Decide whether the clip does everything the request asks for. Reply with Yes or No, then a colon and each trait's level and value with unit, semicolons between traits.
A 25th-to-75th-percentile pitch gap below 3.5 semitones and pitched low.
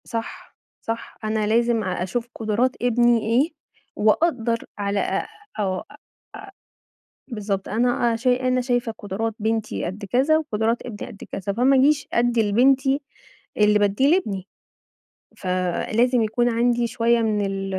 No: average, 2.9 semitones; high, 230 Hz